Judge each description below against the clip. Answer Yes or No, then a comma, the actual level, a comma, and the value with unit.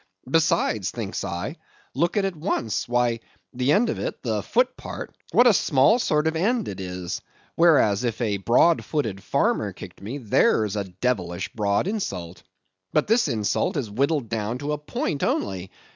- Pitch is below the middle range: Yes, low, 125 Hz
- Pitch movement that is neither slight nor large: No, wide, 7.9 semitones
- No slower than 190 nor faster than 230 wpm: No, average, 165 wpm